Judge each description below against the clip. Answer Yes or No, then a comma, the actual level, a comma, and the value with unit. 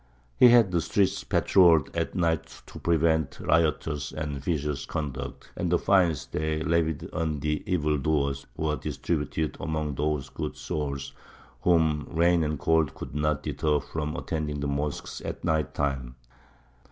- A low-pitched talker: Yes, very low, 75 Hz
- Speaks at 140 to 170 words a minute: Yes, average, 145 wpm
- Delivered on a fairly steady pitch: Yes, narrow, 2.0 semitones